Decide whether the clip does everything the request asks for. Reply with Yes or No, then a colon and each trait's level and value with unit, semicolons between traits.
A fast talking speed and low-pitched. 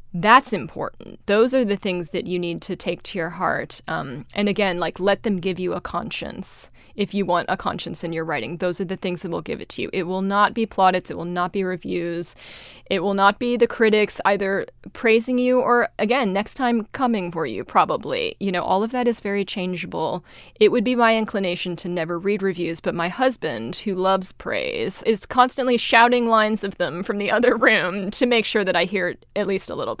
No: fast, 230 wpm; high, 200 Hz